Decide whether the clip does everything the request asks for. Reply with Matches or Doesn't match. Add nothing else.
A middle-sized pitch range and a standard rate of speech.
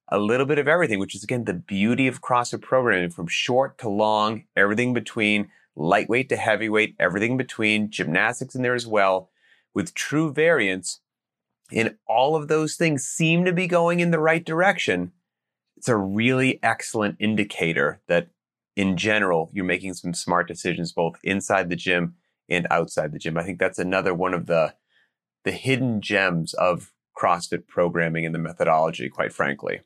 Doesn't match